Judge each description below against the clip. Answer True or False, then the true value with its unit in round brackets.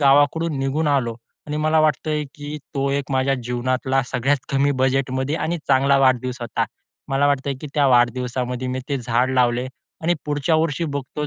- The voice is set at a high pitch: False (135 Hz)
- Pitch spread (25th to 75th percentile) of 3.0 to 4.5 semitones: False (2.4 semitones)